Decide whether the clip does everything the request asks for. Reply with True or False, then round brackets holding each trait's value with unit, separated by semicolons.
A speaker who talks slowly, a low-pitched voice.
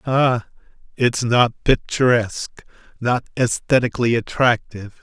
True (85 wpm; 120 Hz)